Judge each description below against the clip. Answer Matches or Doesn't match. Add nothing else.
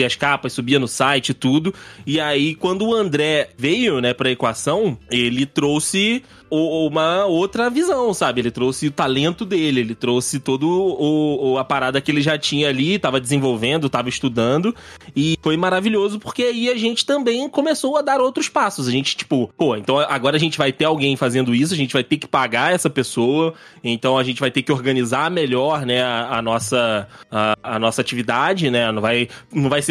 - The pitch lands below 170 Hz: Matches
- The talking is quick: Matches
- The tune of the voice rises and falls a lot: Doesn't match